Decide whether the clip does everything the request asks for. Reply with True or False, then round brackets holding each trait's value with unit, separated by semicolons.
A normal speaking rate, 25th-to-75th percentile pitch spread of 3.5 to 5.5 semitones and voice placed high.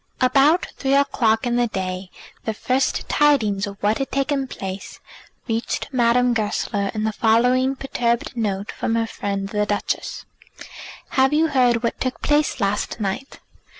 True (150 wpm; 4.3 semitones; 235 Hz)